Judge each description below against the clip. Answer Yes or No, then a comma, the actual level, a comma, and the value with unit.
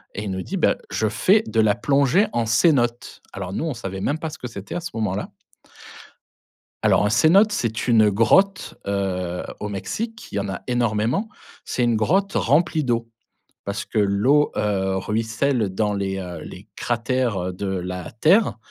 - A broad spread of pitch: Yes, wide, 6.0 semitones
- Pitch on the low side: Yes, low, 110 Hz